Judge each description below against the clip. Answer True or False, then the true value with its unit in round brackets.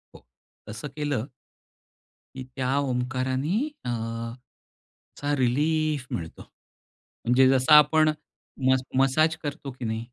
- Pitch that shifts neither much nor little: True (3.1 semitones)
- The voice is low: True (130 Hz)